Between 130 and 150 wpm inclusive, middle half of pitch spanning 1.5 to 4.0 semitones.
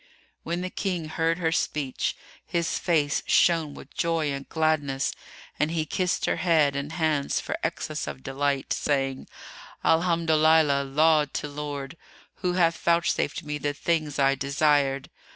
Yes: slow, 135 wpm; average, 2.7 semitones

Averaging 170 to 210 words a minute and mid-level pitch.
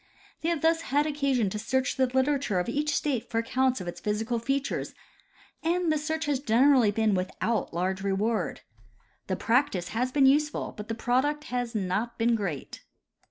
No: average, 175 wpm; very high, 250 Hz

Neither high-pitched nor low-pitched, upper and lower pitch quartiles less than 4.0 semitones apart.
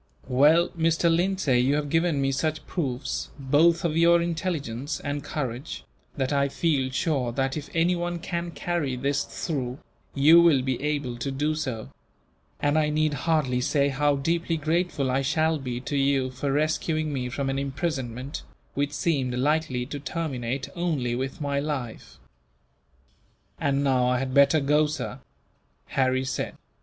Yes: medium, 145 Hz; average, 3.3 semitones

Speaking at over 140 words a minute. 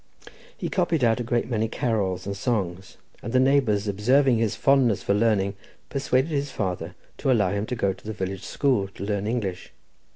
Yes: average, 190 wpm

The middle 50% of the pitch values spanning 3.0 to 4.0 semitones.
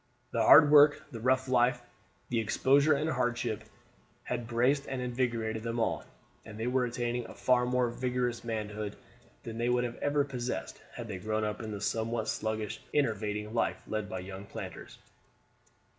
No: narrow, 2.5 semitones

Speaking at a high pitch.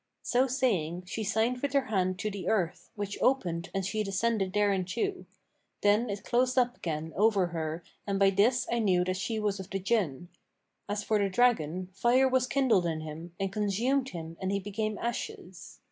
Yes: high, 200 Hz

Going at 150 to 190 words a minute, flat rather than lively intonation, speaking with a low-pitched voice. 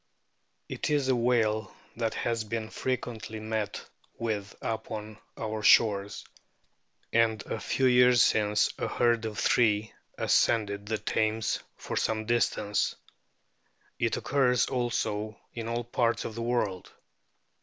No: slow, 135 wpm; narrow, 1.8 semitones; low, 110 Hz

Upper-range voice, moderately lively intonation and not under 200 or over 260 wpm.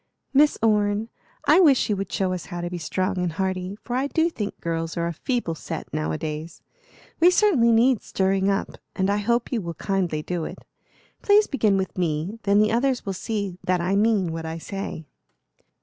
Yes: high, 195 Hz; average, 4.7 semitones; fast, 205 wpm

